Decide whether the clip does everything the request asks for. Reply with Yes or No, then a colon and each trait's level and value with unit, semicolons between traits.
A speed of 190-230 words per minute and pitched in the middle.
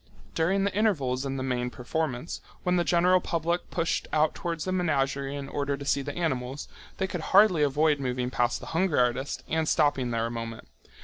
Yes: average, 195 wpm; medium, 145 Hz